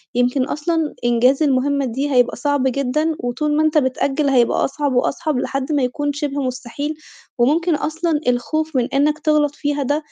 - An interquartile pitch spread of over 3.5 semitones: No, average, 2.9 semitones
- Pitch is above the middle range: Yes, very high, 285 Hz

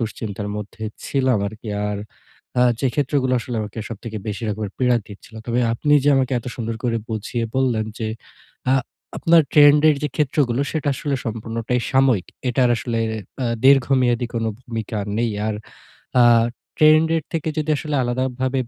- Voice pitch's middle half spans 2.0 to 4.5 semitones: Yes, average, 3.3 semitones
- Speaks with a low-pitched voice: Yes, low, 125 Hz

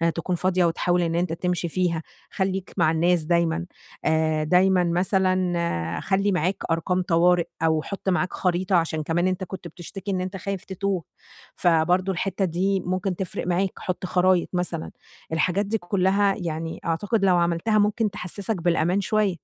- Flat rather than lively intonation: Yes, narrow, 2.2 semitones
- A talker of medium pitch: Yes, medium, 180 Hz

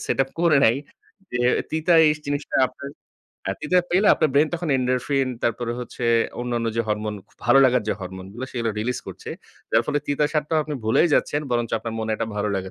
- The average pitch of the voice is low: Yes, low, 125 Hz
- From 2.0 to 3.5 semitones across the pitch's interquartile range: No, average, 4.3 semitones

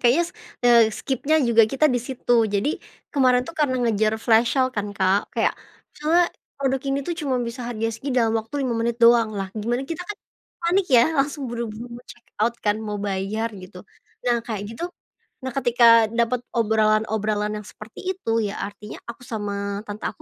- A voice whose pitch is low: No, high, 230 Hz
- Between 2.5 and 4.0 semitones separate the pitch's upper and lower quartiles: Yes, average, 3.3 semitones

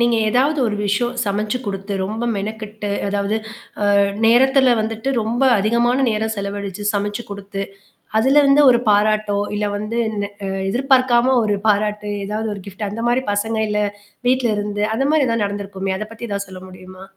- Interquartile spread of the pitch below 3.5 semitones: Yes, average, 2.8 semitones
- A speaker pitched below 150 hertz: No, high, 215 Hz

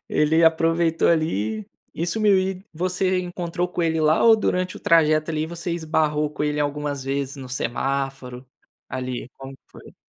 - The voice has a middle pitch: Yes, medium, 155 Hz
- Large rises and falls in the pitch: No, average, 3.8 semitones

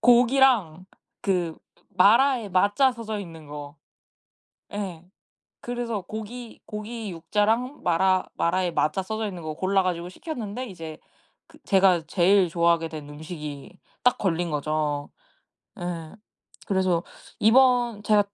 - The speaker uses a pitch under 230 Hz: Yes, high, 190 Hz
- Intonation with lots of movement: No, average, 4.9 semitones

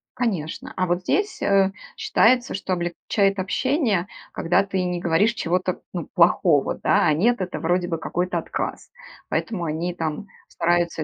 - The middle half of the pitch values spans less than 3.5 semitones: Yes, narrow, 2.6 semitones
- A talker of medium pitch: Yes, medium, 180 Hz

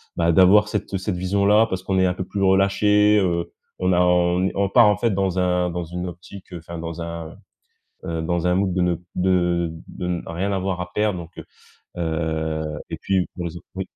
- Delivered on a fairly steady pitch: Yes, narrow, 2.1 semitones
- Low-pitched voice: Yes, very low, 90 Hz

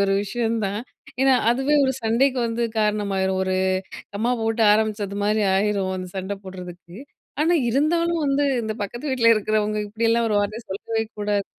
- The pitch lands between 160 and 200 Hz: No, high, 215 Hz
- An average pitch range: Yes, average, 3.0 semitones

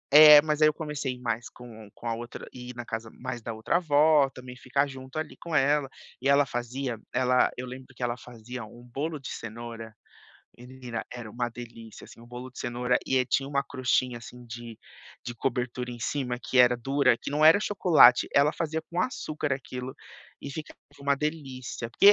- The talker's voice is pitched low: Yes, low, 125 Hz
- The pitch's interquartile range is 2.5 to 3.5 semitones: Yes, average, 2.9 semitones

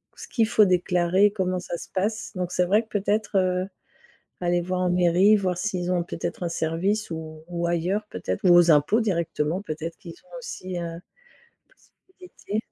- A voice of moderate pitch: Yes, medium, 180 Hz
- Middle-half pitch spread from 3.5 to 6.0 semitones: No, average, 2.9 semitones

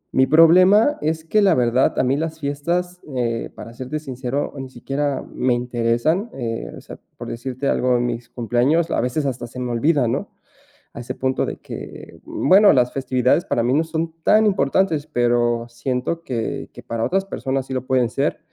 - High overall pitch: No, low, 130 Hz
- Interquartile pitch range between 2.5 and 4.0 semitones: No, average, 4.8 semitones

